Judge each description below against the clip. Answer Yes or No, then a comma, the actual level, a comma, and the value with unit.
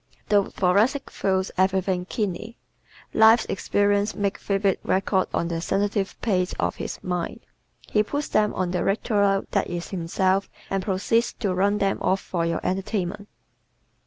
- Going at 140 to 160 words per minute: Yes, average, 150 wpm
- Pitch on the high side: Yes, high, 195 Hz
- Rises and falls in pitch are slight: Yes, narrow, 1.9 semitones